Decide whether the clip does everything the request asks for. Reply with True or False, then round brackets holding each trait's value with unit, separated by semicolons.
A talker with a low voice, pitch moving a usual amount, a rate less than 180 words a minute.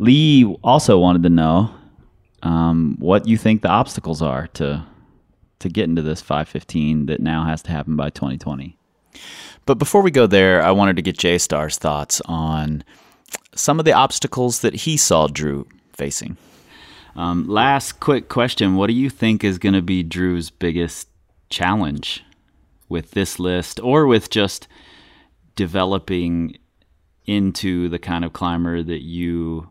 True (85 Hz; 3.5 semitones; 155 wpm)